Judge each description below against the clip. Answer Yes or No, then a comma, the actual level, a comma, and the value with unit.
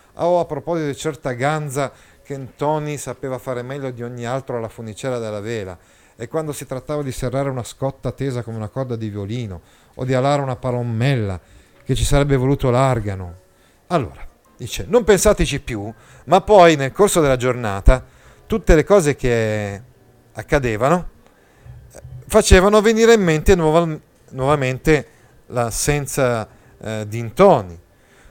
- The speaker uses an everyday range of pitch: Yes, average, 4.2 semitones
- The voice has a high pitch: No, low, 130 Hz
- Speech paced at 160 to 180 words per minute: No, average, 145 wpm